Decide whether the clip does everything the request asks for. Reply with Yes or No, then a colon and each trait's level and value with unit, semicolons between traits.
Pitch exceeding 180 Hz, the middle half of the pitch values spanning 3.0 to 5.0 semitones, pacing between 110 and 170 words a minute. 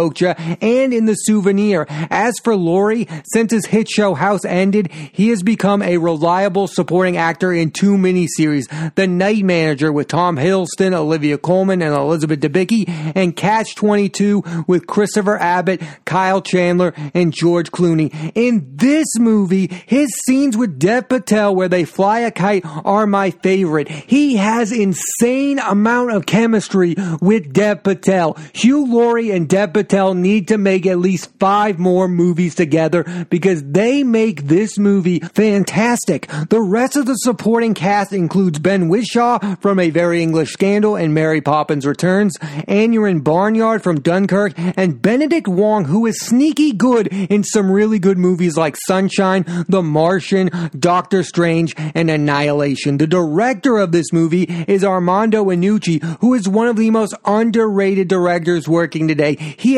Yes: high, 190 Hz; average, 3.7 semitones; average, 150 wpm